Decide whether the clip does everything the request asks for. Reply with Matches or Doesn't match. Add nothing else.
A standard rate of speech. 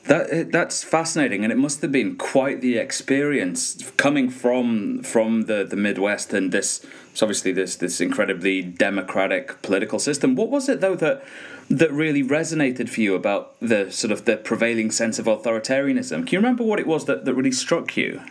Matches